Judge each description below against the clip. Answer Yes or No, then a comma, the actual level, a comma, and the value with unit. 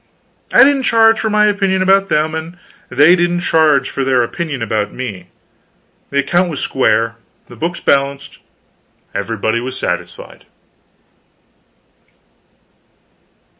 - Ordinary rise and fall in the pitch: No, wide, 6.6 semitones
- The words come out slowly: Yes, slow, 120 wpm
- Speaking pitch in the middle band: Yes, medium, 150 Hz